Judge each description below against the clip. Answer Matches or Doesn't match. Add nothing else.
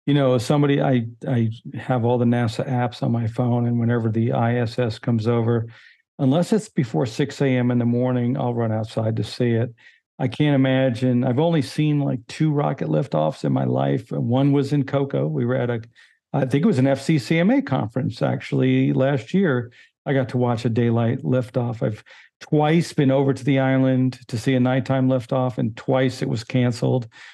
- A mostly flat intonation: Matches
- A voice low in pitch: Matches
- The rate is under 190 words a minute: Doesn't match